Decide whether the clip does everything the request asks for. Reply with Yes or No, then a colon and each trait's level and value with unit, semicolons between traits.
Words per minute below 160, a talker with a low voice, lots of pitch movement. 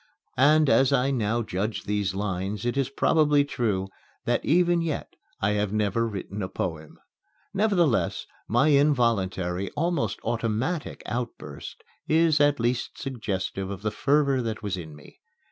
Yes: average, 145 wpm; low, 115 Hz; wide, 6.1 semitones